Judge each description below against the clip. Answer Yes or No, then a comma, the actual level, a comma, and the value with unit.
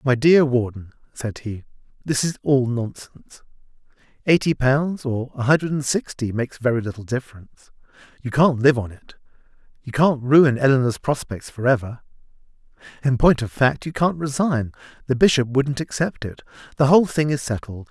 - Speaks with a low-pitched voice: Yes, low, 130 Hz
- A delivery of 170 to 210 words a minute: No, average, 160 wpm